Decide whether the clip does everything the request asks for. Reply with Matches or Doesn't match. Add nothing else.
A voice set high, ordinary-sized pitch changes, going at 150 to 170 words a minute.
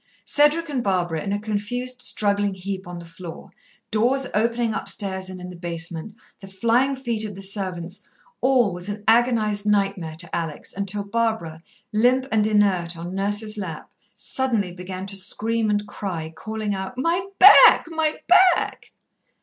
Matches